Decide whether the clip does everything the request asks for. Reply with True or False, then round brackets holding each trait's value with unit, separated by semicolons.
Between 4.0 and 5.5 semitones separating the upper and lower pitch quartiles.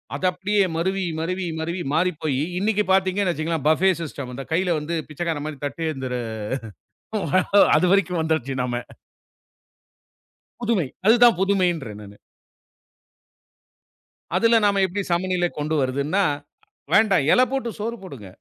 True (4.6 semitones)